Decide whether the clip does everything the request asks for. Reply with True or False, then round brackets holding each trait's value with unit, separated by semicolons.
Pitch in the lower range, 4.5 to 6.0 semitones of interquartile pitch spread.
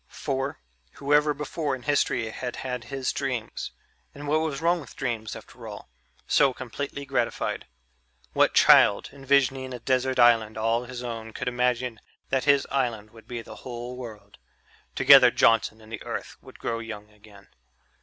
False (125 Hz; 3.2 semitones)